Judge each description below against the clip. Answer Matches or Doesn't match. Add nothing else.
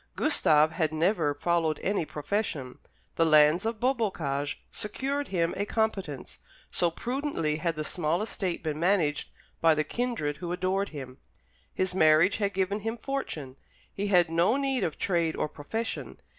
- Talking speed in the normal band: Matches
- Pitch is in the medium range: Matches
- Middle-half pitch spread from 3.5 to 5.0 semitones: Doesn't match